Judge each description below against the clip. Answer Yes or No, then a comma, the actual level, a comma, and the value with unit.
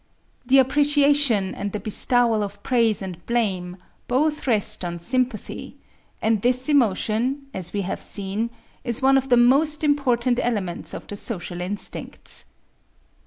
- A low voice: No, high, 235 Hz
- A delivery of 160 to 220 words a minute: No, average, 140 wpm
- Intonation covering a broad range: No, average, 4.6 semitones